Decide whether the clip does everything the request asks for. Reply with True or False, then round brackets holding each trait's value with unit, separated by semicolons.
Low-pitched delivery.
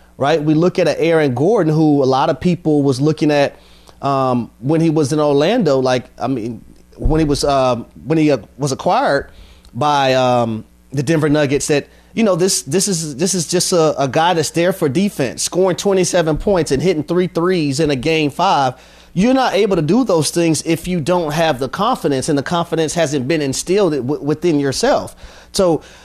False (155 Hz)